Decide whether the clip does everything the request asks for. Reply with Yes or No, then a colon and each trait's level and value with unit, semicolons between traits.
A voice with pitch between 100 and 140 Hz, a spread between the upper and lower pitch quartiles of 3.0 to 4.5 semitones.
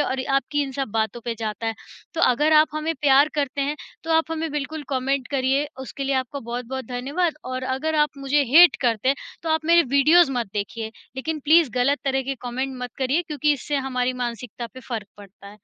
No: very high, 270 Hz; average, 3.4 semitones